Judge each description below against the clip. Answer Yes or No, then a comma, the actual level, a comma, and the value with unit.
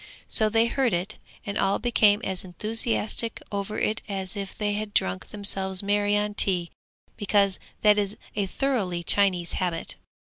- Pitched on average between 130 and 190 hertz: No, high, 205 Hz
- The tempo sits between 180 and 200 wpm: No, average, 155 wpm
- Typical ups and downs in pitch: No, narrow, 2.0 semitones